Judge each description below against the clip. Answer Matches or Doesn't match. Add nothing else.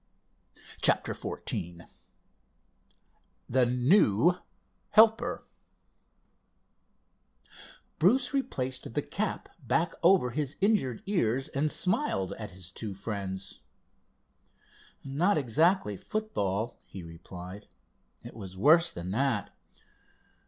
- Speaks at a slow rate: Matches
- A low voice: Matches